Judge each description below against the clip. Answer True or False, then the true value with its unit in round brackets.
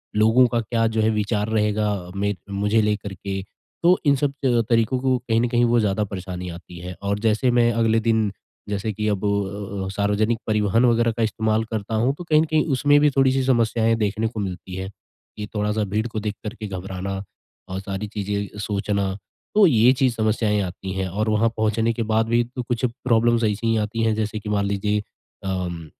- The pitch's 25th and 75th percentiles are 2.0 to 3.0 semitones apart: True (2.4 semitones)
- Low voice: True (110 Hz)